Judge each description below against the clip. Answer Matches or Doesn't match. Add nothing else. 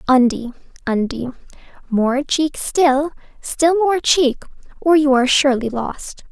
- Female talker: Matches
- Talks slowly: Matches